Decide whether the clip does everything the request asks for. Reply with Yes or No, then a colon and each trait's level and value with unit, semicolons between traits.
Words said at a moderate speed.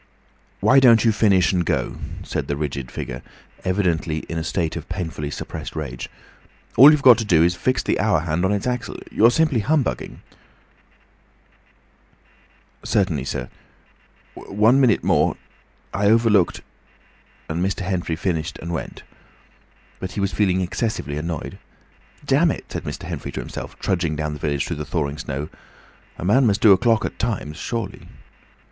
Yes: average, 160 wpm